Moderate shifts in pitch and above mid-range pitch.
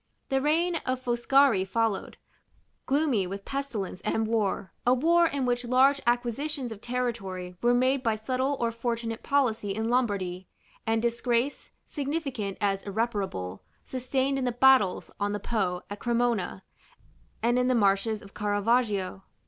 Yes: average, 4.1 semitones; high, 235 Hz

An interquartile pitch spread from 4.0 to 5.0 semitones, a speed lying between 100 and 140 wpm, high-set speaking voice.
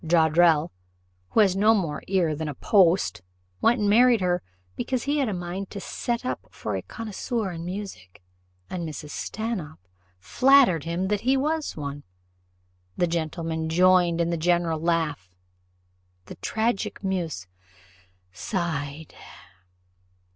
No: average, 4.6 semitones; slow, 135 wpm; medium, 175 Hz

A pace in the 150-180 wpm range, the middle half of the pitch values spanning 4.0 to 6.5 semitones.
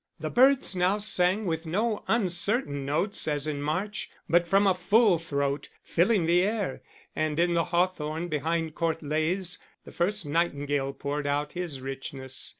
Yes: average, 155 wpm; average, 4.3 semitones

